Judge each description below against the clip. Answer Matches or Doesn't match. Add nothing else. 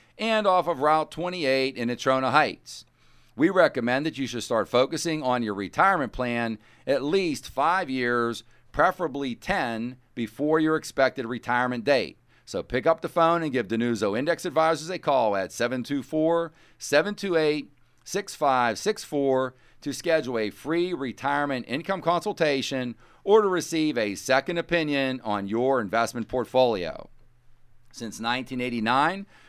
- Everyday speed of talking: Doesn't match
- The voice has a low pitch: Matches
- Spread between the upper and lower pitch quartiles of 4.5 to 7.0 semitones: Matches